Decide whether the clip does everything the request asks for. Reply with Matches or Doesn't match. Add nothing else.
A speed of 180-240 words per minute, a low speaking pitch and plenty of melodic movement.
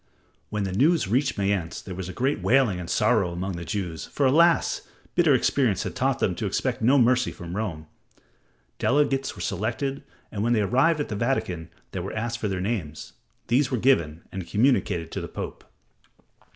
Matches